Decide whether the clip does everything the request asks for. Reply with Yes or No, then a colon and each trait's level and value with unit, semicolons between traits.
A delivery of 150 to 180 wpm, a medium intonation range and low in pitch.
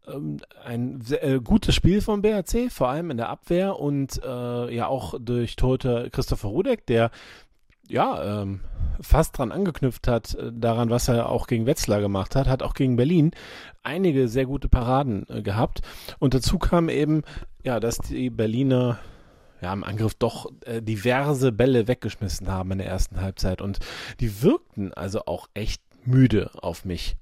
Yes: average, 165 wpm; average, 4.6 semitones; low, 120 Hz